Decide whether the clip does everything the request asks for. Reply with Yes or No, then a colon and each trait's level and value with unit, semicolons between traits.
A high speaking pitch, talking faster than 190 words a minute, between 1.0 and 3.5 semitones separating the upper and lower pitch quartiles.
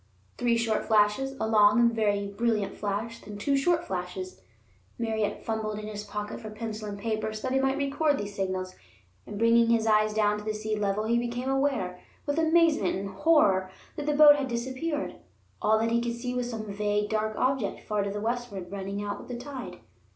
Yes: high, 220 Hz; average, 200 wpm; average, 3.0 semitones